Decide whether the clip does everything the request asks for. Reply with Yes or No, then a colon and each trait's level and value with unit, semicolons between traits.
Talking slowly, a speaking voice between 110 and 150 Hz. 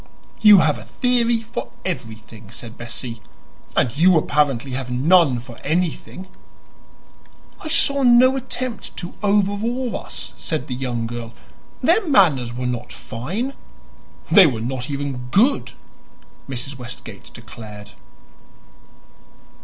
Yes: slow, 120 wpm; medium, 140 Hz